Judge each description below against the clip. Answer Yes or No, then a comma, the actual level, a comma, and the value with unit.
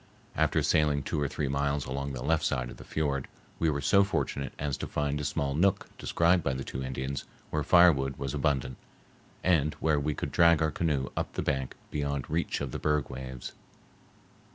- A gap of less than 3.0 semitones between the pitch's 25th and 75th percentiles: Yes, narrow, 2.5 semitones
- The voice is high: No, very low, 70 Hz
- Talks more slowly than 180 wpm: No, average, 200 wpm